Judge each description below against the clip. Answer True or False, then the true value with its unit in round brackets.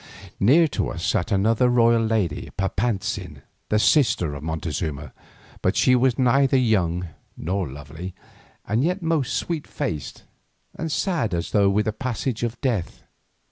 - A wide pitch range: True (6.0 semitones)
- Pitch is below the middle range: True (110 Hz)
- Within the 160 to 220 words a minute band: False (145 wpm)